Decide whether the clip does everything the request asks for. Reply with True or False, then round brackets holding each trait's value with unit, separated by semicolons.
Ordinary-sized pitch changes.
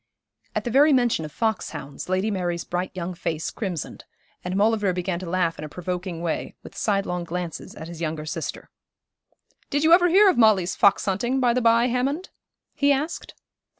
False (5.8 semitones)